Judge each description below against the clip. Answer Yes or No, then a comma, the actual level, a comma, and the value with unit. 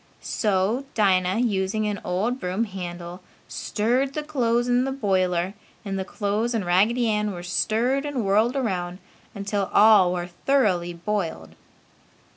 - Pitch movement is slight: No, average, 4.4 semitones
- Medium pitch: No, high, 205 Hz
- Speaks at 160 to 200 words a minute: No, average, 140 wpm